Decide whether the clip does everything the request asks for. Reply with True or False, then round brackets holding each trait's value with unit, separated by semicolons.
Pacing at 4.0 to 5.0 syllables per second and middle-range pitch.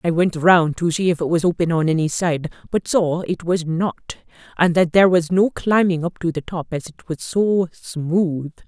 True (4.7 syllables/s; 170 Hz)